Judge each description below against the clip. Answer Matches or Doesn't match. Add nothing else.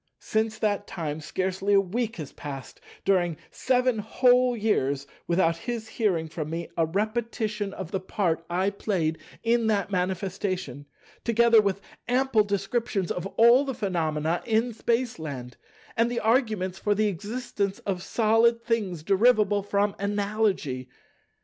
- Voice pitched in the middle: Doesn't match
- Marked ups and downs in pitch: Doesn't match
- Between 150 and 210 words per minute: Doesn't match